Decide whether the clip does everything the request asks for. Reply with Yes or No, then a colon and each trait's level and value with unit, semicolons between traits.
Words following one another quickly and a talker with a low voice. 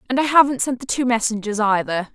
No: fast, 225 wpm; high, 235 Hz